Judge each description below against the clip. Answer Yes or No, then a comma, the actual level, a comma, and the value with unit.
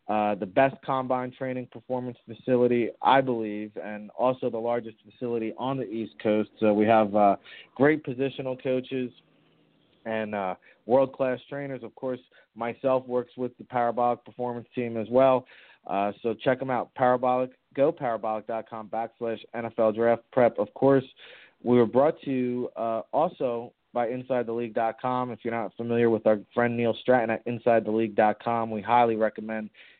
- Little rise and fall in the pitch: Yes, narrow, 2.2 semitones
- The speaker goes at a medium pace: Yes, average, 155 wpm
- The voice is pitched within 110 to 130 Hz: Yes, low, 120 Hz